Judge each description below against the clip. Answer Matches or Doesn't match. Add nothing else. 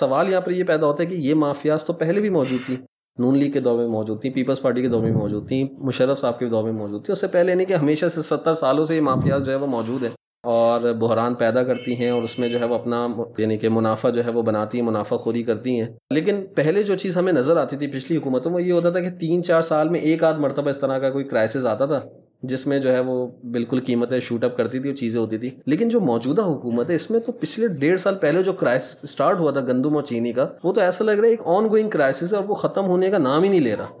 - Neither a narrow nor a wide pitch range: Doesn't match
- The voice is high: Doesn't match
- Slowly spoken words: Doesn't match